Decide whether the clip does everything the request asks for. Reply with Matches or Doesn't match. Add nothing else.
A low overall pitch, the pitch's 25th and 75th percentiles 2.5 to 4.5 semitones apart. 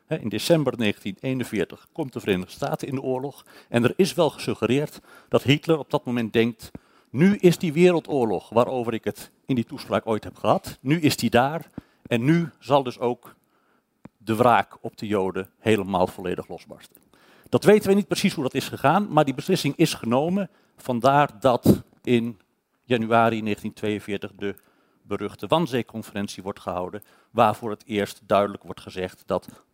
Doesn't match